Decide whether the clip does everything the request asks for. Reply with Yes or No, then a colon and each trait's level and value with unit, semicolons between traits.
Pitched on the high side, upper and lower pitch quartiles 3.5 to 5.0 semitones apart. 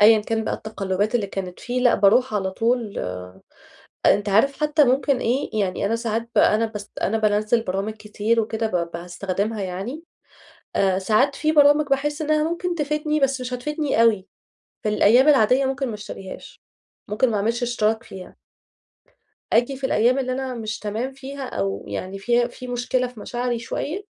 Yes: high, 230 Hz; average, 4.2 semitones